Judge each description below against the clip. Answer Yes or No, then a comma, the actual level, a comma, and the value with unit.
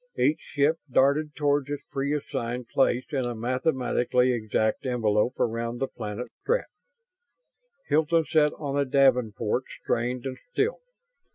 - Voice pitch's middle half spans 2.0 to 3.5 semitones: Yes, average, 3.1 semitones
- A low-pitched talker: Yes, low, 130 Hz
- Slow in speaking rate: Yes, slow, 130 wpm